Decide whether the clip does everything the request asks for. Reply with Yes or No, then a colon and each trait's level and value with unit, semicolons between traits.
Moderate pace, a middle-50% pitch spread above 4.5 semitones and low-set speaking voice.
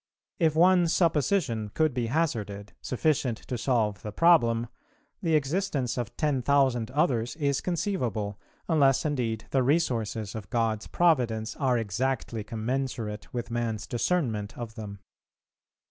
No: slow, 130 wpm; average, 5.2 semitones; low, 125 Hz